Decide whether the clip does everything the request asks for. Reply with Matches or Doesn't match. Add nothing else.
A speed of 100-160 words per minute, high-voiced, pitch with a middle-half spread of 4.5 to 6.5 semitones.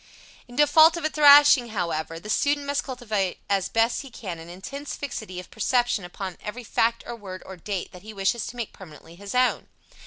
Doesn't match